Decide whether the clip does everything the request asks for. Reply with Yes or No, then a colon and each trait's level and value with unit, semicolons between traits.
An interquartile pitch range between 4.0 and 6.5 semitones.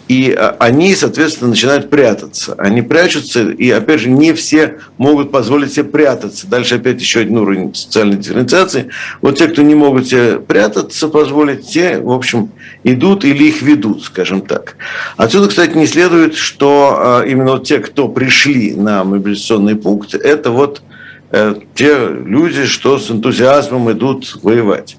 Yes: average, 4.5 semitones